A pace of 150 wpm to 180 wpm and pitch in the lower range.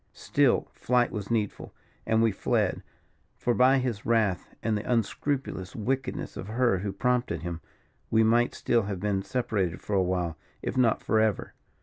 Yes: average, 165 wpm; low, 110 Hz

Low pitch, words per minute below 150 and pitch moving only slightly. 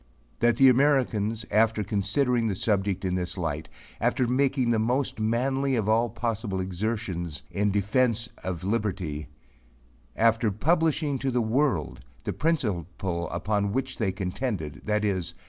No: low, 110 Hz; slow, 135 wpm; average, 4.6 semitones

